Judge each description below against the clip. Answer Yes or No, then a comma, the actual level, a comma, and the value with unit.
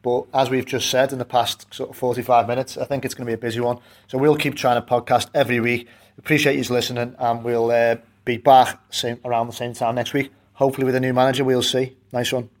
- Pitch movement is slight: Yes, narrow, 1.7 semitones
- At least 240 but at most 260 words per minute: Yes, fast, 250 wpm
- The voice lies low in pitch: Yes, low, 125 Hz